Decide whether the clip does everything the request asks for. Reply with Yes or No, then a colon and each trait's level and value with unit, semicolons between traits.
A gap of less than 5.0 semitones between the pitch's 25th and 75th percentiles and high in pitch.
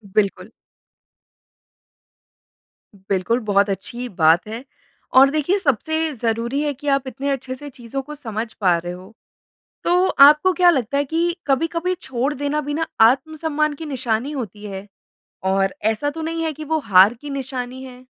No: average, 5.3 semitones; very high, 265 Hz